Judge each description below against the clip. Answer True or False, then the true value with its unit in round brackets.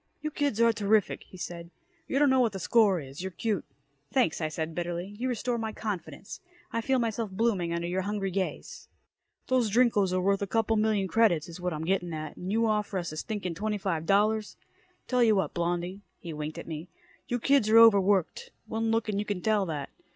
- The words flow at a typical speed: False (215 wpm)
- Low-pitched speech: False (200 Hz)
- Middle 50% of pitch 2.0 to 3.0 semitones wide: False (4.3 semitones)